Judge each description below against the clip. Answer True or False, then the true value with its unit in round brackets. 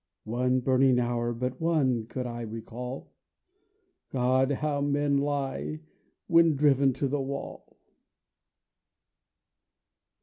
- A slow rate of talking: True (100 wpm)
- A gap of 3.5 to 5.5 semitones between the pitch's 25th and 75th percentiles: False (2.5 semitones)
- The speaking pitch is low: True (130 Hz)